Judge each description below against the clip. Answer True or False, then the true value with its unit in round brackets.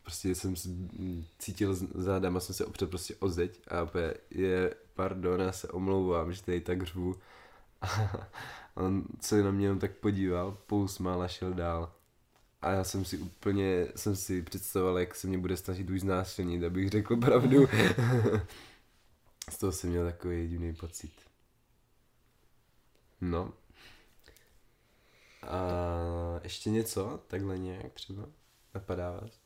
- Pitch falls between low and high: False (95 Hz)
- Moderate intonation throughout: False (1.7 semitones)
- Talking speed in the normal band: True (140 wpm)